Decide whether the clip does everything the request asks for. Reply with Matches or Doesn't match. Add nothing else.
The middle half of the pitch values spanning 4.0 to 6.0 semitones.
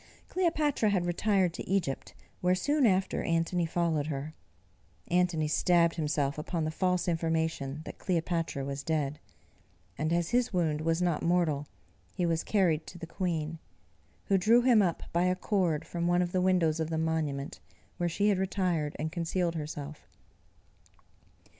Doesn't match